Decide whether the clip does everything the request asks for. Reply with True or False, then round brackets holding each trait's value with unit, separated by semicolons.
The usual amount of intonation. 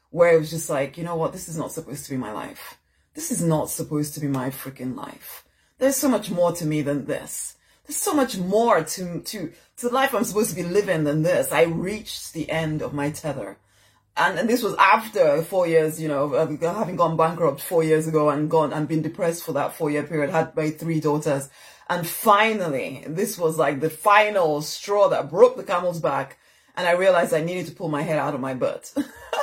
True (3.9 semitones)